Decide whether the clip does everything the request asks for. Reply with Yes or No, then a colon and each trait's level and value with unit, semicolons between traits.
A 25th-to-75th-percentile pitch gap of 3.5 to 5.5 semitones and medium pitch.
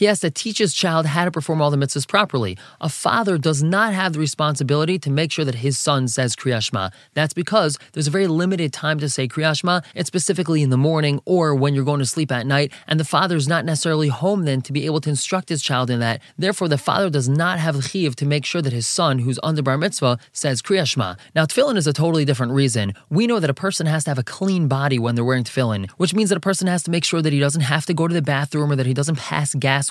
Yes: average, 3.9 semitones; medium, 150 Hz